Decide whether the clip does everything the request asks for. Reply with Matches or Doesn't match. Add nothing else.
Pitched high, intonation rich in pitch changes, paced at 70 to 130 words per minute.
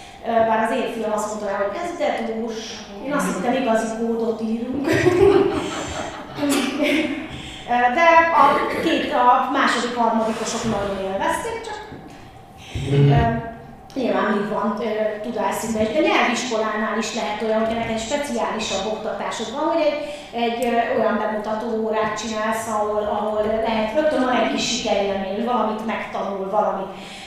Doesn't match